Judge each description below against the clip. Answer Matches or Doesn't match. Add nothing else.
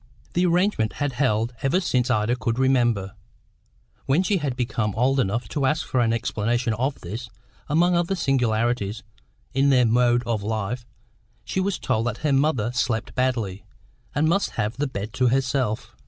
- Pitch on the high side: Doesn't match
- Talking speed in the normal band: Matches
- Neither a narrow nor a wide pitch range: Matches